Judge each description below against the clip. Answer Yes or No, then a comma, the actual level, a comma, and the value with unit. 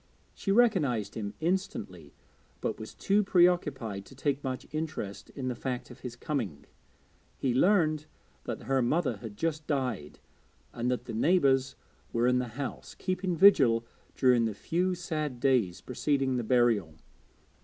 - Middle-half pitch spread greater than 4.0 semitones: Yes, average, 5.3 semitones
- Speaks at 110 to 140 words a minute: No, average, 155 wpm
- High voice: No, low, 130 Hz